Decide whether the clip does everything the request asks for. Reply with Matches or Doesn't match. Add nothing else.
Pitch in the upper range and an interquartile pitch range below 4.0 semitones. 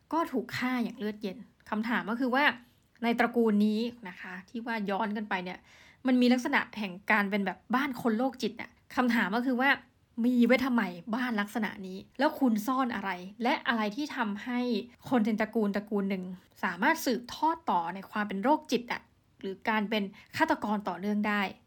Matches